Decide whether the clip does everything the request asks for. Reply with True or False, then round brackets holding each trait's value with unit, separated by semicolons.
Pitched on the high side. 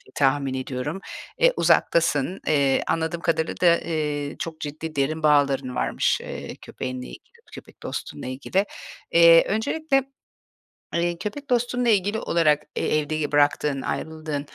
False (155 Hz)